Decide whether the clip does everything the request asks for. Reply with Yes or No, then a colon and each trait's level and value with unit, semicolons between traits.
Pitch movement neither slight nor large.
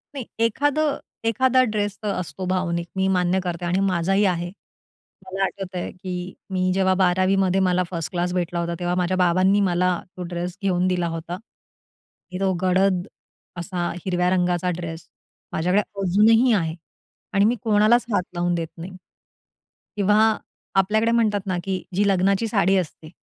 No: narrow, 2.0 semitones